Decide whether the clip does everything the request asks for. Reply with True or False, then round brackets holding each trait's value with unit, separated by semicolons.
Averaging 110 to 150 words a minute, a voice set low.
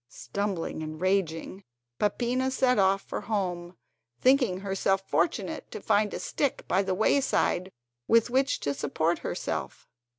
False (135 wpm; 195 Hz)